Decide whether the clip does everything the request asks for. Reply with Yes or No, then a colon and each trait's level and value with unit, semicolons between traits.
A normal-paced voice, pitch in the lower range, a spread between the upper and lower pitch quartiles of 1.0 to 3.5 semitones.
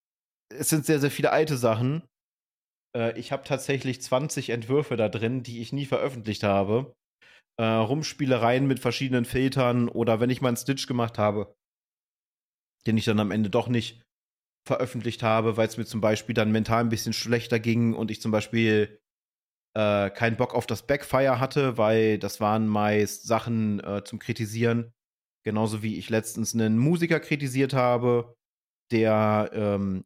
Yes: average, 165 wpm; low, 115 Hz; average, 2.8 semitones